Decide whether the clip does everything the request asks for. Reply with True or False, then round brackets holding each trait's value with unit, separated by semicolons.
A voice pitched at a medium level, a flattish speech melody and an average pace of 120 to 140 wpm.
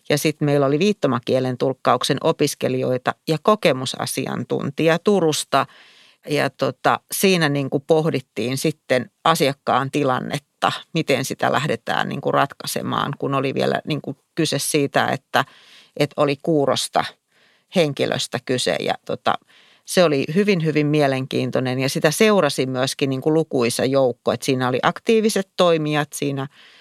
False (145 Hz; 3.2 semitones; 125 wpm)